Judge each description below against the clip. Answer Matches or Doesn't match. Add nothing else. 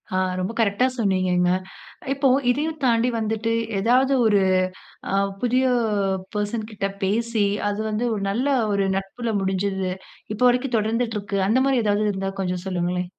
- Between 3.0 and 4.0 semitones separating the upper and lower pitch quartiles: Matches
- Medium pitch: Doesn't match